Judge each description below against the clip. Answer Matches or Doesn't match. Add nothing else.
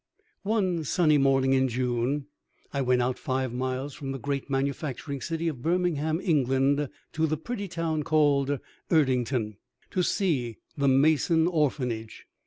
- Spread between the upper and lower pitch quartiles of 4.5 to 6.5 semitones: Doesn't match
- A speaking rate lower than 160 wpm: Matches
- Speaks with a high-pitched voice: Doesn't match